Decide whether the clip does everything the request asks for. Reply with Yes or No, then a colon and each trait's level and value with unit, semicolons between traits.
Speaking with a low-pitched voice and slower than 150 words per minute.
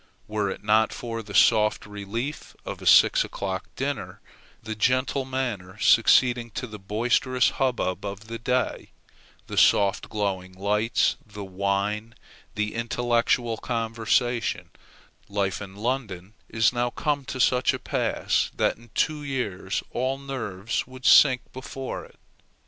Yes: low, 115 Hz; average, 140 wpm